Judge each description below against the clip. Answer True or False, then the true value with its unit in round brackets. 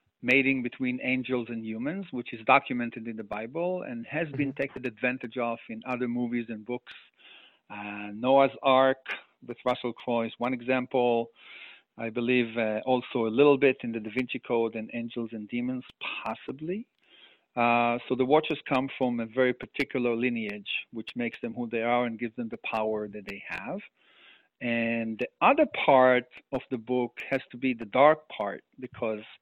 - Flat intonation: True (2.0 semitones)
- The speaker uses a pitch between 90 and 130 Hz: True (125 Hz)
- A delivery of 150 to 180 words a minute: True (175 wpm)